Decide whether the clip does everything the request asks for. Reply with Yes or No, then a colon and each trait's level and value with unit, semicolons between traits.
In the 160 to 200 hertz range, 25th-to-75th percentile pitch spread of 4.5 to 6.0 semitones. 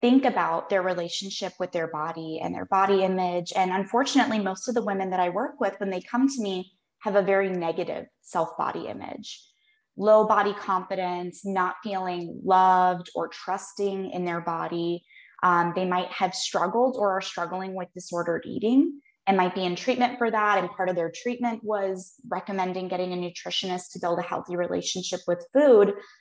No: high, 190 Hz; average, 2.7 semitones